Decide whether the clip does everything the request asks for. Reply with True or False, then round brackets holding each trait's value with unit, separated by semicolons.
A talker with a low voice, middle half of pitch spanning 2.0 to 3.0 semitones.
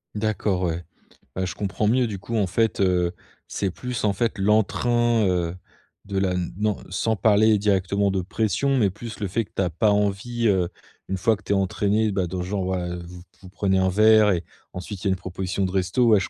True (100 Hz; 2.6 semitones)